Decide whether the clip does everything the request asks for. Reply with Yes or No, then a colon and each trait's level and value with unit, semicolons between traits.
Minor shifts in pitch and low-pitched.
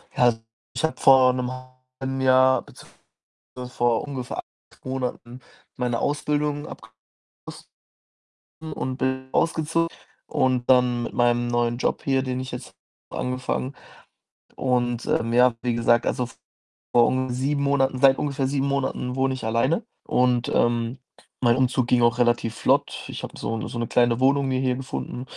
Yes: narrow, 1.7 semitones; low, 130 Hz